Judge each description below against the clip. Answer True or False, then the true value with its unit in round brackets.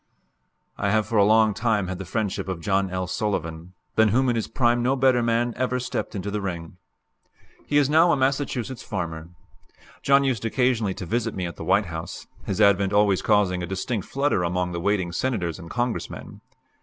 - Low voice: True (105 Hz)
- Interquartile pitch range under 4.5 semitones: False (4.8 semitones)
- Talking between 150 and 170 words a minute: False (195 wpm)